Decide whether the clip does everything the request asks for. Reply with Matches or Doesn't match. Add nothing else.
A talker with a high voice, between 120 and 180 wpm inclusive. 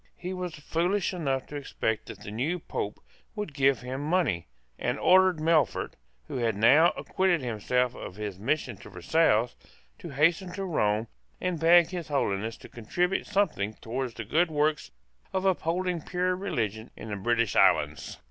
Doesn't match